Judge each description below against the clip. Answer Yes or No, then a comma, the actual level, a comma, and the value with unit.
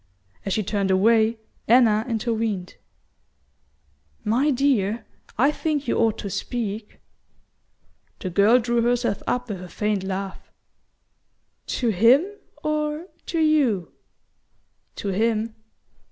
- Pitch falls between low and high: No, high, 225 Hz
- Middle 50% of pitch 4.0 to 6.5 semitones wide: No, average, 3.5 semitones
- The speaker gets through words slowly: Yes, slow, 110 wpm